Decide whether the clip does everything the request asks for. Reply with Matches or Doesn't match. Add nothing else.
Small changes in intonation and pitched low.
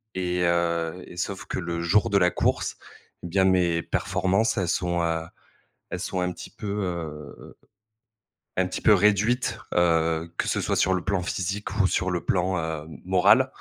Matches